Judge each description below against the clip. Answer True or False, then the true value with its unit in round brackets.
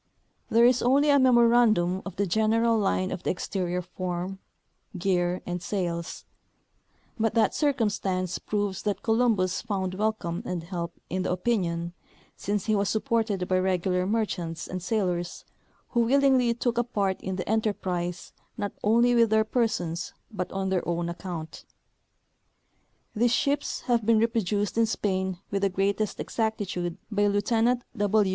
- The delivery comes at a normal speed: True (150 wpm)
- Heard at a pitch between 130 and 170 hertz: False (200 Hz)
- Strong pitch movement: False (3.8 semitones)